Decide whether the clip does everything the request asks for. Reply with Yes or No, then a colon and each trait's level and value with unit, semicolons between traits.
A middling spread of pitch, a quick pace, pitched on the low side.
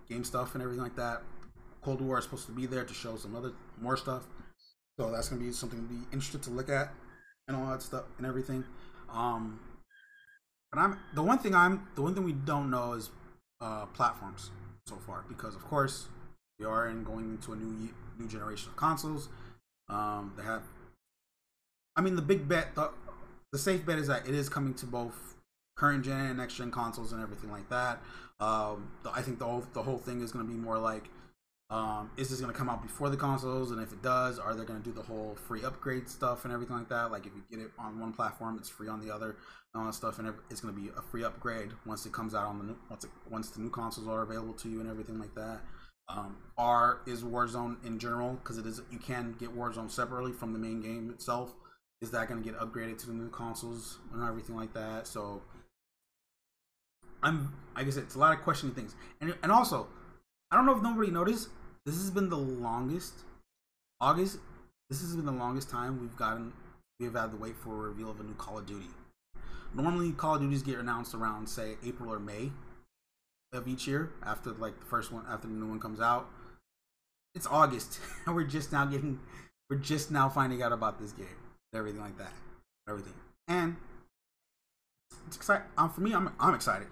Yes: average, 3.0 semitones; fast, 220 wpm; low, 120 Hz